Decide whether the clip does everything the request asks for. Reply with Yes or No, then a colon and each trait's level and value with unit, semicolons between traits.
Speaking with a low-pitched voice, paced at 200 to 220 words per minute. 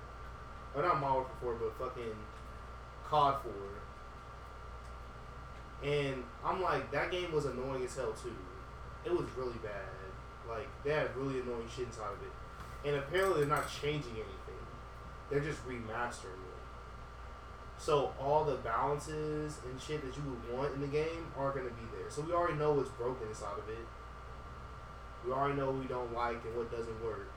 No: low, 120 Hz; average, 175 wpm